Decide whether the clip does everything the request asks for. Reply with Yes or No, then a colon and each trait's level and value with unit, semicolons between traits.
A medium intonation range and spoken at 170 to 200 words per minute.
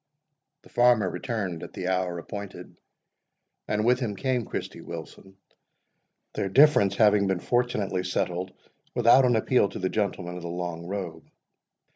No: average, 4.4 semitones; average, 145 wpm